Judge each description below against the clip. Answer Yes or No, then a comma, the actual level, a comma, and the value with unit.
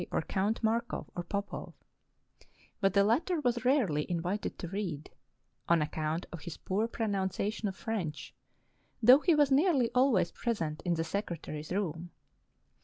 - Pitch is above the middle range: Yes, high, 200 Hz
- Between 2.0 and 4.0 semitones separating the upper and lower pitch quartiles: No, wide, 5.5 semitones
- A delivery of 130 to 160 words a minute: Yes, average, 150 wpm